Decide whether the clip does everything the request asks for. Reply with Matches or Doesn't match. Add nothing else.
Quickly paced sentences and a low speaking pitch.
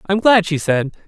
Doesn't match